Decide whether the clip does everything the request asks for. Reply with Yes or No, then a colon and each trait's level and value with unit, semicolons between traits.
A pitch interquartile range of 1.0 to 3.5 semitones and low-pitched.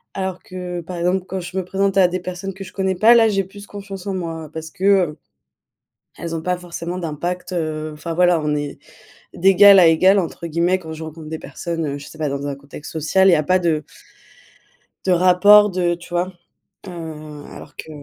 No: average, 2.9 semitones; medium, 175 Hz